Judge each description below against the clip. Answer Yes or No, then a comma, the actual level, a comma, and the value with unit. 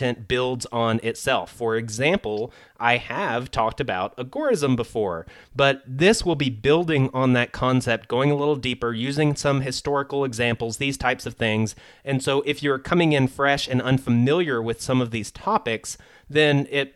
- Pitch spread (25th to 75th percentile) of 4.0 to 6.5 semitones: No, average, 3.0 semitones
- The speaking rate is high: No, average, 165 wpm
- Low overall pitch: Yes, low, 130 Hz